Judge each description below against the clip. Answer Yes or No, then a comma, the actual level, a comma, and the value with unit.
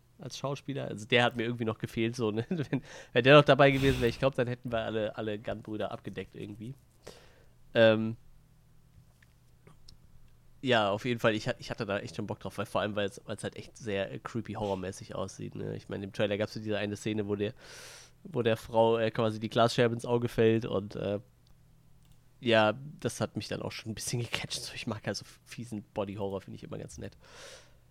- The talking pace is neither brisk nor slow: No, fast, 215 wpm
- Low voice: Yes, low, 115 Hz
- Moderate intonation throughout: Yes, average, 3.0 semitones